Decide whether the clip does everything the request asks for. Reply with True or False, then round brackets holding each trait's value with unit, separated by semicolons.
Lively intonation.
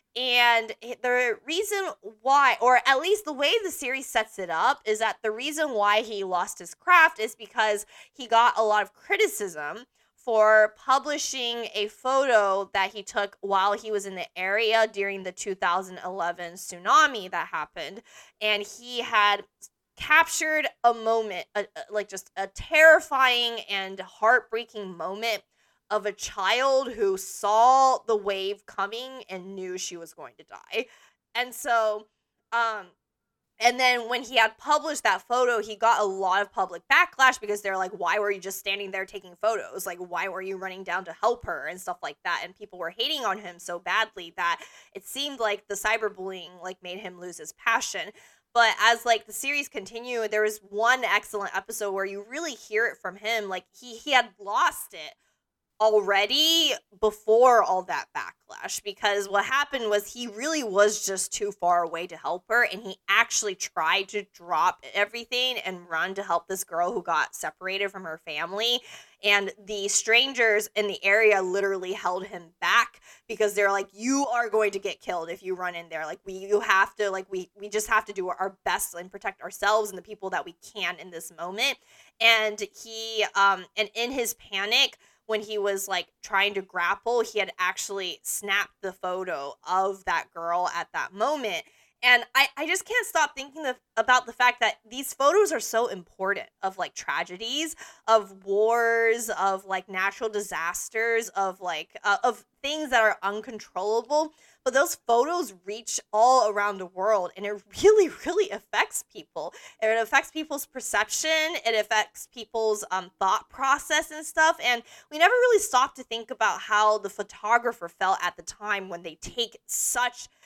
False (3.9 semitones)